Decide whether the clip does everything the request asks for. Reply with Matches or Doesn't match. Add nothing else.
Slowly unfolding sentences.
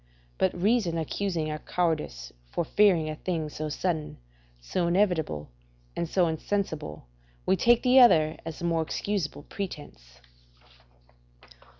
Matches